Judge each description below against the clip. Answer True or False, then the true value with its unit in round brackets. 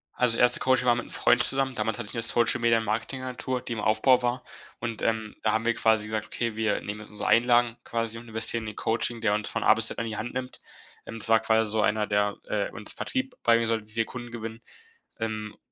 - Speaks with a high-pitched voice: False (115 Hz)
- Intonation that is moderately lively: False (1.8 semitones)